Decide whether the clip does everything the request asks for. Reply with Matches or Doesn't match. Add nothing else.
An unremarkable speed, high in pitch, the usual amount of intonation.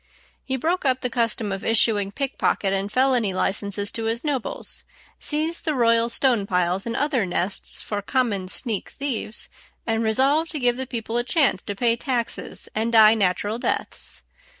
Matches